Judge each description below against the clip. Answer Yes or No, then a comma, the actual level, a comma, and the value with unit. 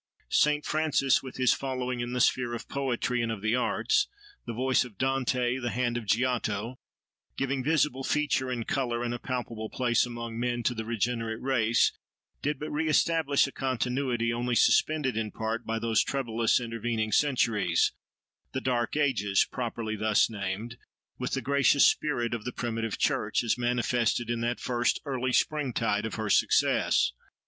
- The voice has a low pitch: Yes, low, 120 Hz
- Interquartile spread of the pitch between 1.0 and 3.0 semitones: Yes, narrow, 2.5 semitones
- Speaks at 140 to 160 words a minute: Yes, average, 155 wpm